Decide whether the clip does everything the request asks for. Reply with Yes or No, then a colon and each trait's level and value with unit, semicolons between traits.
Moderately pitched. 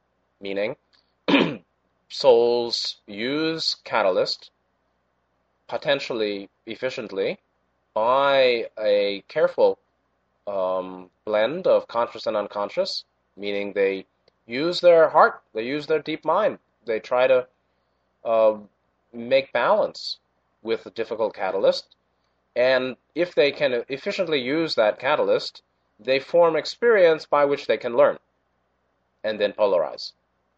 No: low, 115 Hz